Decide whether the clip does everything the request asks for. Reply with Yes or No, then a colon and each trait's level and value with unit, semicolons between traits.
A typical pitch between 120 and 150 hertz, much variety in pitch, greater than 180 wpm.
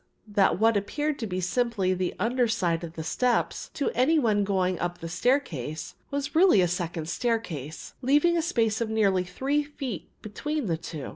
No: high, 210 Hz; wide, 6.7 semitones; average, 200 wpm